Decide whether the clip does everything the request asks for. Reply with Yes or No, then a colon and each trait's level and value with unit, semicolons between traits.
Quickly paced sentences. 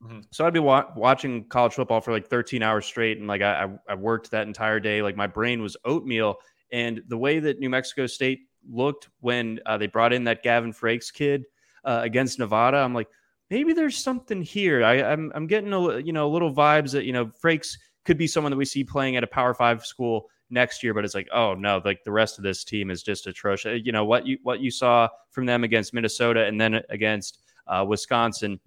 Yes: fast, 225 wpm